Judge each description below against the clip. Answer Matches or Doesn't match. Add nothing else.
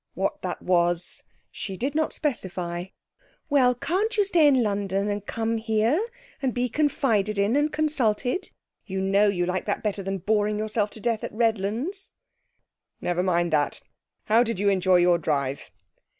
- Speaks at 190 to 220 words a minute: Doesn't match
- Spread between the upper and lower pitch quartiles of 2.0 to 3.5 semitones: Doesn't match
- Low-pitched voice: Doesn't match